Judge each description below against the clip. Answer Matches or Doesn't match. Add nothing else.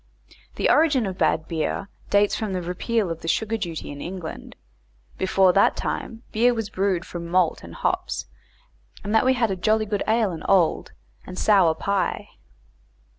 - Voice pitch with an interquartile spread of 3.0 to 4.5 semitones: Matches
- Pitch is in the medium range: Doesn't match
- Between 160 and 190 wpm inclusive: Matches